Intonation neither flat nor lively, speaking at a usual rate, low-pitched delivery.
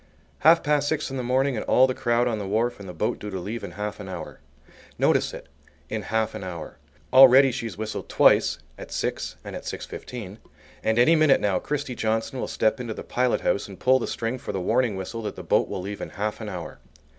No: average, 3.8 semitones; fast, 240 wpm; low, 115 Hz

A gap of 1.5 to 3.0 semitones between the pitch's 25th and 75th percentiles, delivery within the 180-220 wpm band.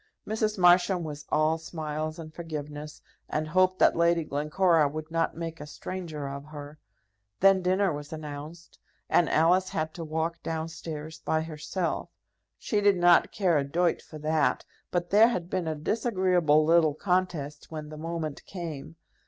No: average, 2.7 semitones; average, 160 wpm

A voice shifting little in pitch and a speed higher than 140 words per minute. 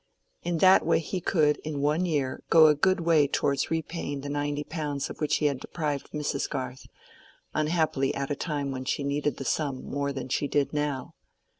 Yes: narrow, 2.1 semitones; average, 195 wpm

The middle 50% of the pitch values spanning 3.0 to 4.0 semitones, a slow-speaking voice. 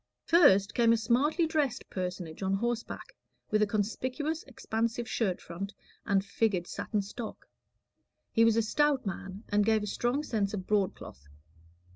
No: average, 3.5 semitones; average, 150 wpm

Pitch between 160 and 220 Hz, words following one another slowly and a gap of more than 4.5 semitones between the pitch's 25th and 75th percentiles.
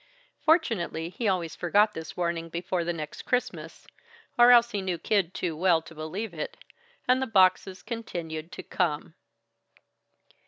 No: medium, 185 Hz; average, 150 wpm; average, 5.1 semitones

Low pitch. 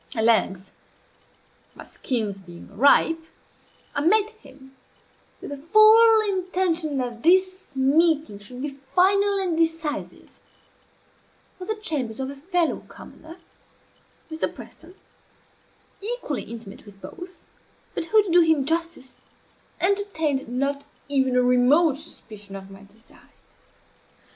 No: very high, 305 Hz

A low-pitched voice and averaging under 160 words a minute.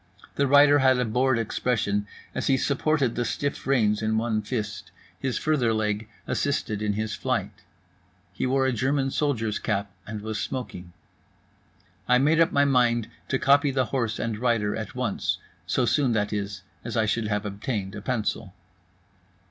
No: low, 115 Hz; average, 170 wpm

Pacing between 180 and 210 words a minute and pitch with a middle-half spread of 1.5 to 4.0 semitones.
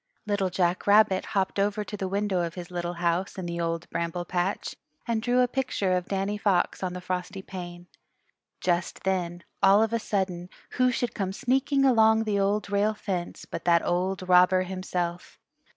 Yes: average, 185 wpm; average, 2.8 semitones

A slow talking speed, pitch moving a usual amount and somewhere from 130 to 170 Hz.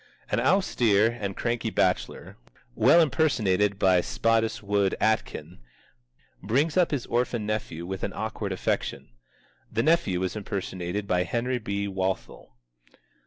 No: slow, 120 wpm; average, 4.0 semitones; low, 105 Hz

